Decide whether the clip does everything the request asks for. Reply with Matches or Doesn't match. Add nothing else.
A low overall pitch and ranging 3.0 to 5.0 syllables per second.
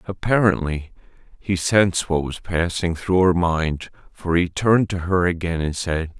Matches